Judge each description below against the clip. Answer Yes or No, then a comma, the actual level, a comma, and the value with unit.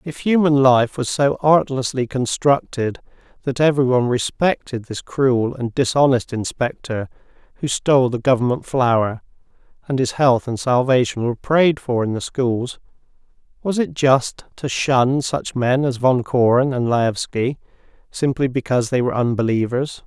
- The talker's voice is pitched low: Yes, low, 130 Hz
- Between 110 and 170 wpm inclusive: Yes, average, 145 wpm